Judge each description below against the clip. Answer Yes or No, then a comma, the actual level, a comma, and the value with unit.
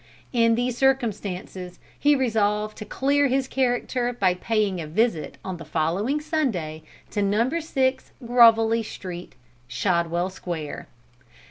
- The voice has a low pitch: No, high, 220 Hz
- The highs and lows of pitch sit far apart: Yes, wide, 5.9 semitones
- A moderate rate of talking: No, slow, 125 wpm